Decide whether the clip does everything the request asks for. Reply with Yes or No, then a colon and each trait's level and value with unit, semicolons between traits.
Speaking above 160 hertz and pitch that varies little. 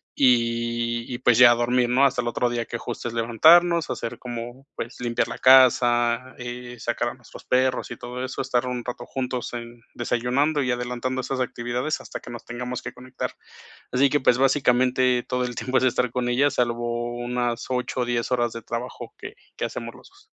No: low, 125 Hz; narrow, 1.3 semitones